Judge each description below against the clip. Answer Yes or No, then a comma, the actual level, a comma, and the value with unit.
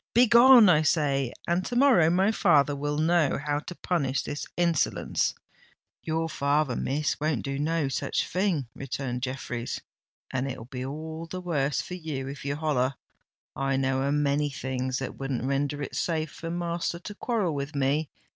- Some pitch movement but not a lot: Yes, average, 3.7 semitones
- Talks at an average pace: Yes, average, 170 wpm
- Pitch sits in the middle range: Yes, medium, 145 Hz